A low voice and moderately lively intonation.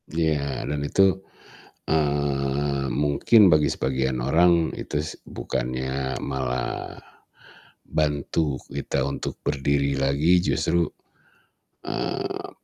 No: very low, 70 Hz; narrow, 2.3 semitones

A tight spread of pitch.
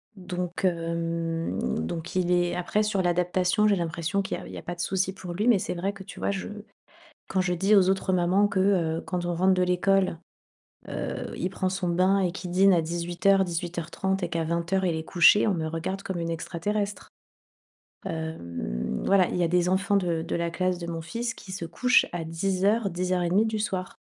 Yes: narrow, 2.3 semitones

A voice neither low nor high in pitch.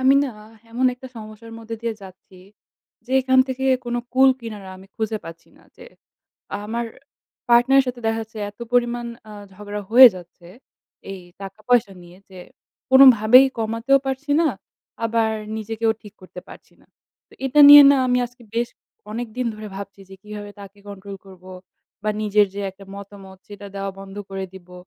No: high, 220 Hz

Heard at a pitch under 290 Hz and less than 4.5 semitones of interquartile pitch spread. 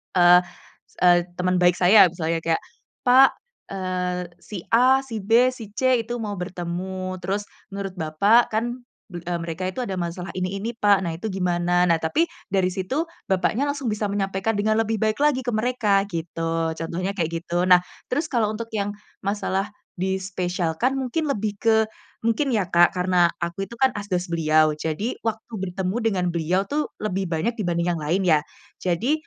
Yes: high, 190 Hz; average, 4.1 semitones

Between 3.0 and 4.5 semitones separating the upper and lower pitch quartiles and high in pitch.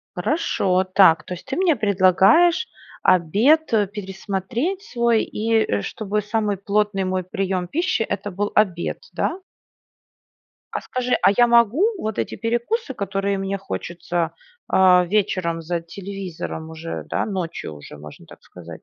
Yes: average, 4.1 semitones; high, 195 Hz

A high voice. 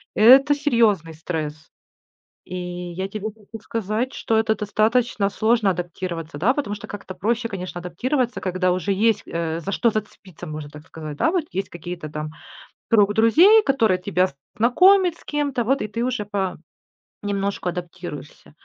Yes: high, 200 Hz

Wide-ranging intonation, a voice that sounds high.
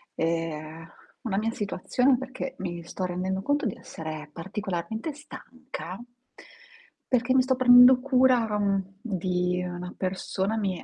Yes: wide, 6.0 semitones; high, 195 Hz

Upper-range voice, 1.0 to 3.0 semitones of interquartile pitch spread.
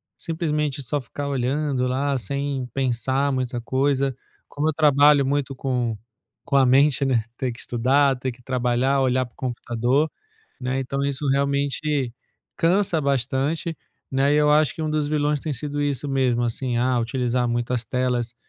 No: low, 135 Hz; narrow, 2.4 semitones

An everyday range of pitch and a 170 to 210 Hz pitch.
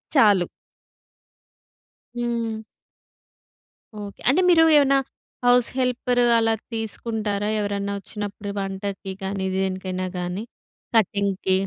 Yes: average, 3.3 semitones; high, 205 Hz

